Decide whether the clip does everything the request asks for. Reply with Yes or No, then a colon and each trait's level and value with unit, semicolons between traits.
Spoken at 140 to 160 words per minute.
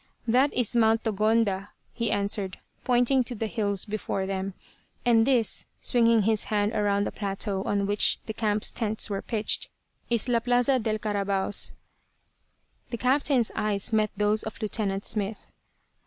Yes: average, 150 wpm